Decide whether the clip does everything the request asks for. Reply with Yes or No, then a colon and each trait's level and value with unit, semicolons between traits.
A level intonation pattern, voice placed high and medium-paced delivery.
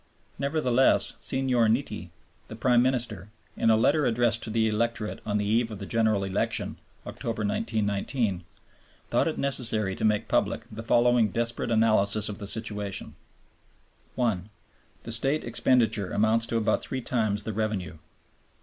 No: narrow, 2.2 semitones; low, 110 Hz; average, 150 wpm